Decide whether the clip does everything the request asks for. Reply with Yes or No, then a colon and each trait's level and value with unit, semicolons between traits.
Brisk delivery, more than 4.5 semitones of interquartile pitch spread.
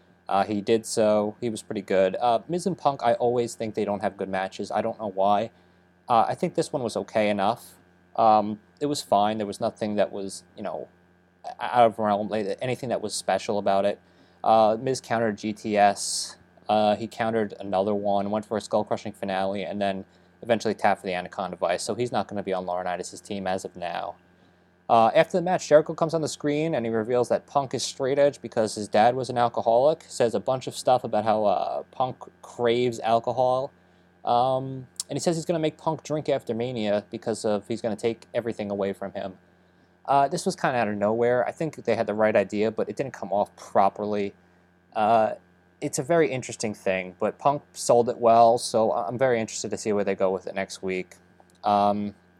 No: fast, 220 wpm; average, 4.0 semitones